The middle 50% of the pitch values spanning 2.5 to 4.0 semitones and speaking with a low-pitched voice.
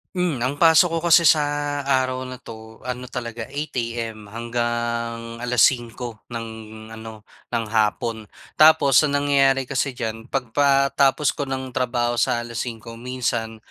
Yes: average, 2.9 semitones; low, 125 Hz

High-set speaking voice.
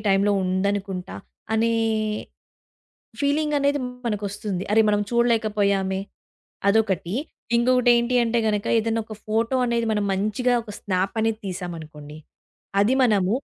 Yes: high, 210 Hz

